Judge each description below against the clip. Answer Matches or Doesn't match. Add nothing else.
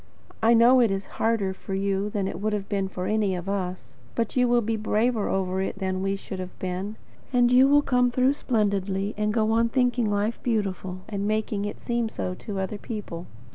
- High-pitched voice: Matches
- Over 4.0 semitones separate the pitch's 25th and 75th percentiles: Doesn't match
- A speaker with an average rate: Doesn't match